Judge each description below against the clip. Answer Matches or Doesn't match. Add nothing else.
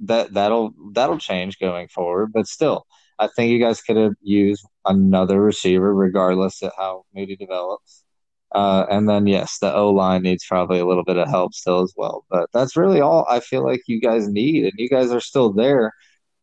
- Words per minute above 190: Matches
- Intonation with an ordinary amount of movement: Doesn't match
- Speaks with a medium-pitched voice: Doesn't match